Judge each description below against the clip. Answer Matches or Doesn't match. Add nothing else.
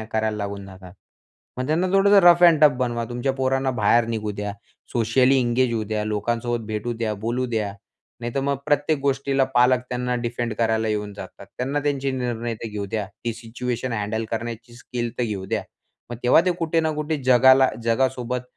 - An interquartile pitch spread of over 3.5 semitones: Doesn't match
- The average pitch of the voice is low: Matches